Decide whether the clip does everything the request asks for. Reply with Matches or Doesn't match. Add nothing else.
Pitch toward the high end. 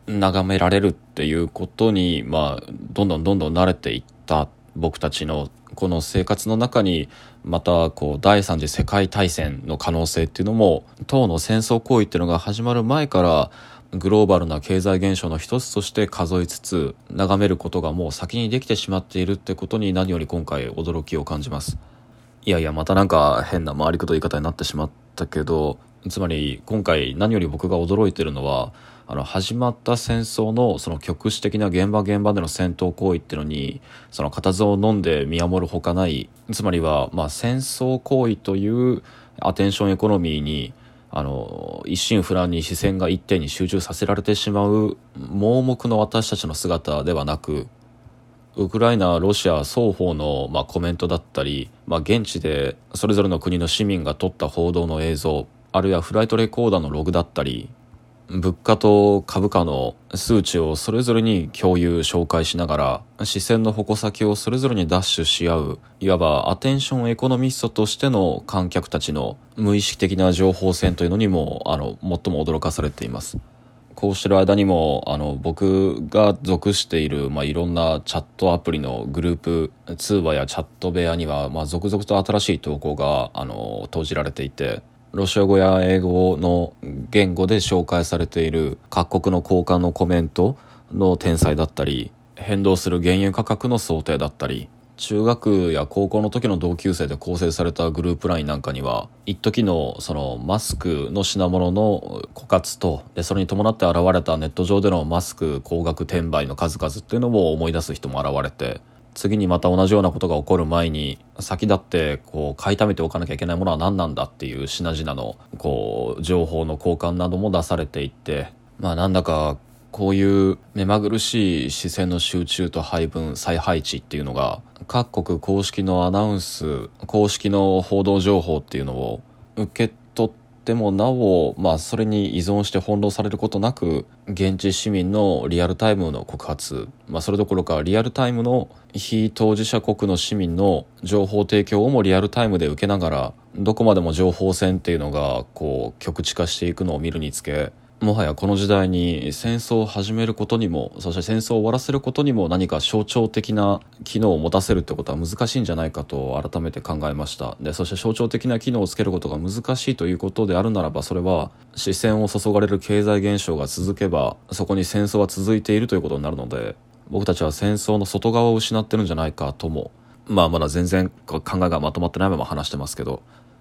Doesn't match